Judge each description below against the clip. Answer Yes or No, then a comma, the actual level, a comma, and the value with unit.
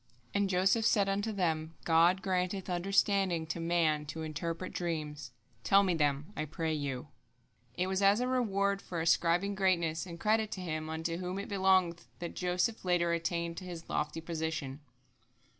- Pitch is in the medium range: Yes, medium, 175 Hz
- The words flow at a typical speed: Yes, average, 165 wpm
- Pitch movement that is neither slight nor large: Yes, average, 3.1 semitones